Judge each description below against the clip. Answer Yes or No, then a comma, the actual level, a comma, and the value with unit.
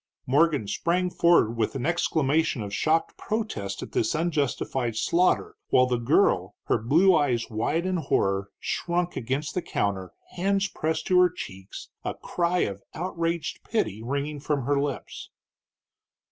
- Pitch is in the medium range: Yes, medium, 150 Hz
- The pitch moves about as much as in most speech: No, wide, 6.9 semitones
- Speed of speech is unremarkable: Yes, average, 145 wpm